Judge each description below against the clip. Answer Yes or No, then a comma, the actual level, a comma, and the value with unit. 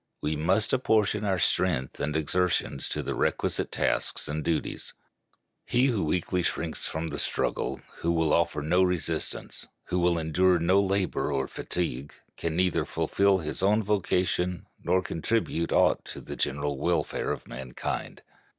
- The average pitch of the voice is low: Yes, very low, 85 Hz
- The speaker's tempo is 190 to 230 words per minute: No, average, 150 wpm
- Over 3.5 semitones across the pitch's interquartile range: No, average, 3.1 semitones